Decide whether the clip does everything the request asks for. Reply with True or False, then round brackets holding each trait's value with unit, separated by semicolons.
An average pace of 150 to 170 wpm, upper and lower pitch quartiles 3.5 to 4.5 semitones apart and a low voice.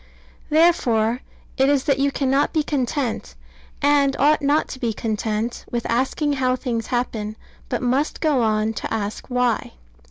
False (155 wpm; 3.9 semitones; 255 Hz)